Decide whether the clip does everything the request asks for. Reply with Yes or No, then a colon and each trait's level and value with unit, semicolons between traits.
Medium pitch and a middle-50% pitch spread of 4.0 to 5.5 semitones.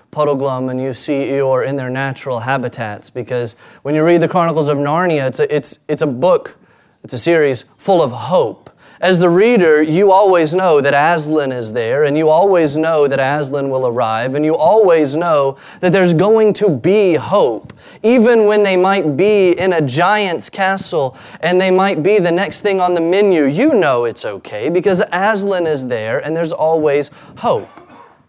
Yes: medium, 160 Hz; average, 5.1 semitones